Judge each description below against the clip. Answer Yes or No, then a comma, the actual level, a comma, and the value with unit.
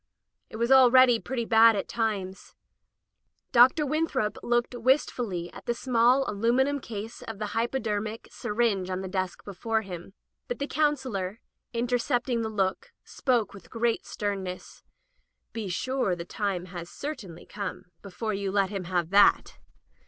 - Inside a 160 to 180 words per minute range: No, average, 150 wpm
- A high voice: Yes, high, 225 Hz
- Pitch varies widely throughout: No, average, 4.0 semitones